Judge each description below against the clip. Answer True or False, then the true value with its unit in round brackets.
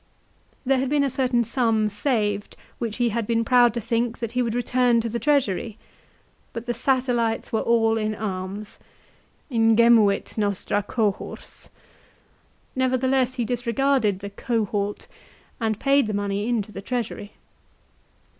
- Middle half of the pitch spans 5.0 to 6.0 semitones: False (2.8 semitones)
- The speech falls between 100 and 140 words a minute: False (155 wpm)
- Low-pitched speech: False (230 Hz)